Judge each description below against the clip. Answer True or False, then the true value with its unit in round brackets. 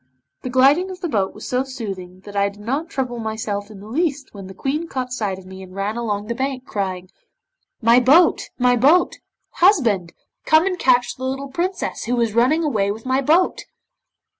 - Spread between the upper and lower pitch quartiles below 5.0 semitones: False (5.3 semitones)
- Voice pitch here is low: False (245 Hz)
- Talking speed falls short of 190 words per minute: False (200 wpm)